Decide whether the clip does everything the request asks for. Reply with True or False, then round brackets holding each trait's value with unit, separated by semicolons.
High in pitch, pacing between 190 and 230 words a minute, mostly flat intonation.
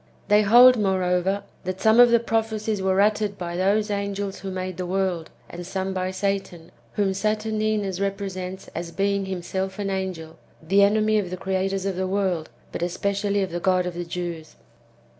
False (195 Hz; 180 wpm; 1.8 semitones)